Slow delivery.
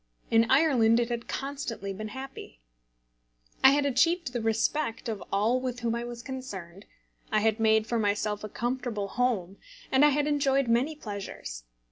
No: average, 165 wpm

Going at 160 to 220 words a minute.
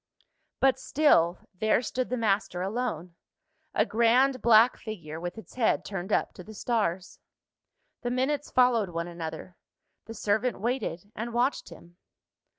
No: average, 145 wpm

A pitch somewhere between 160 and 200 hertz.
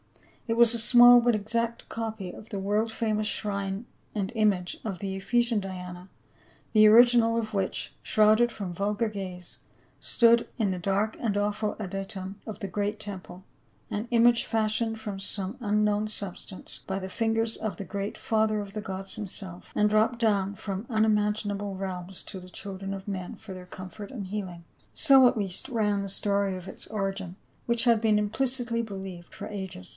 No: high, 210 Hz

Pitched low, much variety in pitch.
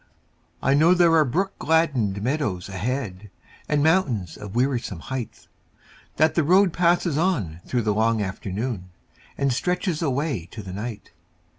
Yes: low, 130 Hz; wide, 7.7 semitones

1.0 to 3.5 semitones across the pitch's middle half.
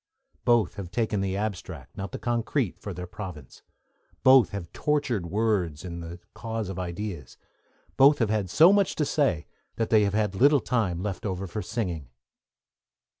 No: average, 4.6 semitones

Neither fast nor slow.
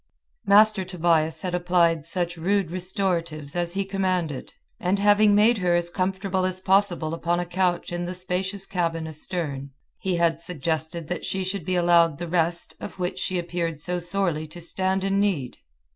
Yes: average, 175 wpm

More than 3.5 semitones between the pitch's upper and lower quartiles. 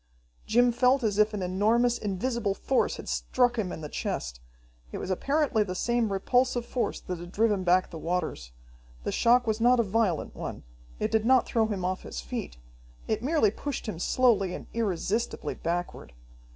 Yes: average, 4.8 semitones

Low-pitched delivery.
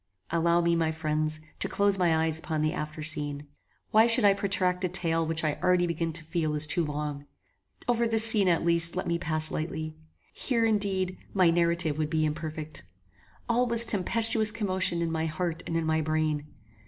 No: medium, 170 Hz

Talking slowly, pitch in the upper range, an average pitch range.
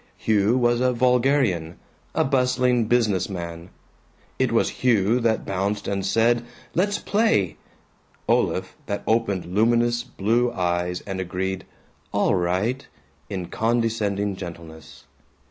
No: slow, 115 wpm; low, 105 Hz; average, 4.3 semitones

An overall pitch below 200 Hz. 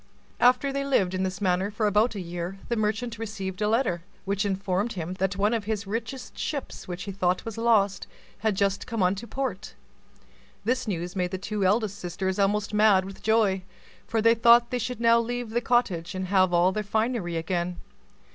No: high, 205 Hz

